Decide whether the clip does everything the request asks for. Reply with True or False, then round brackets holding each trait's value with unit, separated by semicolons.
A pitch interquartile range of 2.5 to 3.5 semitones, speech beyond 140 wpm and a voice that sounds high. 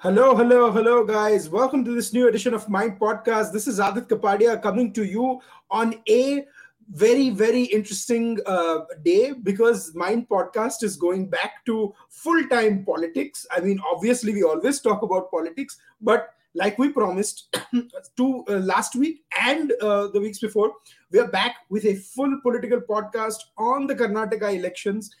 True (3.2 semitones; 160 wpm; 225 Hz)